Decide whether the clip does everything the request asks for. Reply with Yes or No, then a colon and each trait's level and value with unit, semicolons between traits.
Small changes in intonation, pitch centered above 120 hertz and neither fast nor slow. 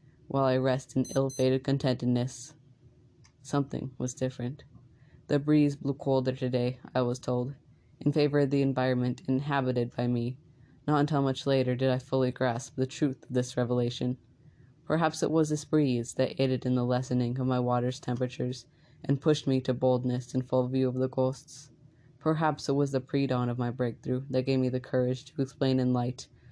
Yes: narrow, 1.9 semitones; low, 130 Hz; average, 185 wpm